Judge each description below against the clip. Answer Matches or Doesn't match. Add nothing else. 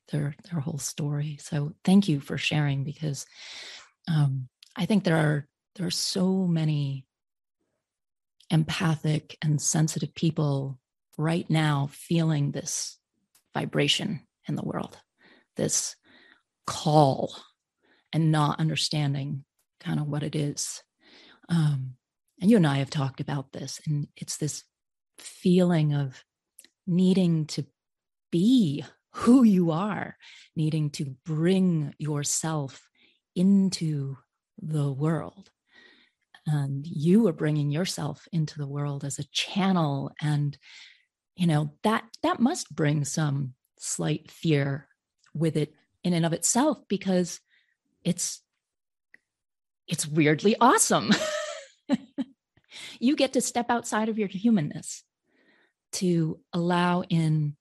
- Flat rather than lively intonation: Doesn't match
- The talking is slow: Matches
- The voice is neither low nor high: Matches